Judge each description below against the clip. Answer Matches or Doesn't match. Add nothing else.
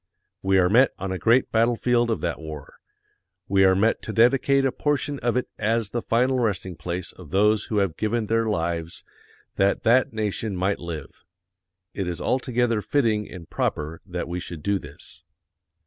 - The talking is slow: Doesn't match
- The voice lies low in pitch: Matches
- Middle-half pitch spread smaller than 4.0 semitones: Doesn't match